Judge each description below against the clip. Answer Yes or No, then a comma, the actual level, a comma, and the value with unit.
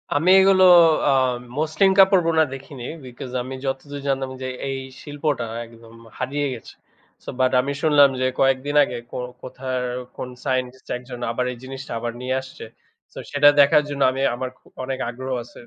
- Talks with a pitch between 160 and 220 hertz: No, low, 135 Hz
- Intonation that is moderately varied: No, narrow, 2.1 semitones